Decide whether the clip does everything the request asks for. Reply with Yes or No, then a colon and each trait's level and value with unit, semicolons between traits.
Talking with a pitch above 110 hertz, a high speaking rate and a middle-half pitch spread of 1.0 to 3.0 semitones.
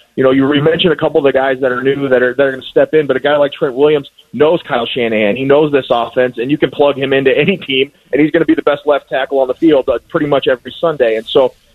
Yes: medium, 140 Hz; fast, 300 wpm; average, 2.7 semitones